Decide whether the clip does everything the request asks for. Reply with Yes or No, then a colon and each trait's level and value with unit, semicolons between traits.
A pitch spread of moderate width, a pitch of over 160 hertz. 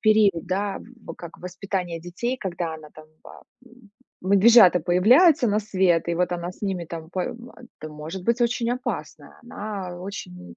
Yes: average, 4.0 semitones; medium, 185 Hz